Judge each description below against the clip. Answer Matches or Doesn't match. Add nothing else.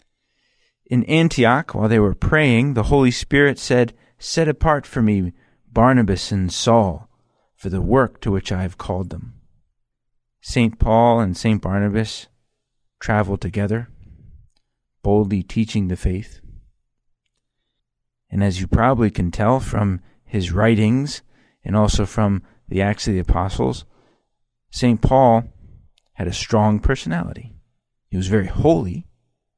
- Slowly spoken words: Matches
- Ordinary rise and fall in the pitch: Matches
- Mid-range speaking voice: Doesn't match